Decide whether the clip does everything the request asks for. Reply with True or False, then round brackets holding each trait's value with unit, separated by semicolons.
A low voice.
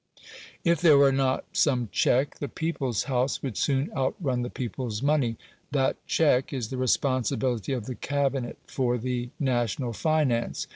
True (130 Hz)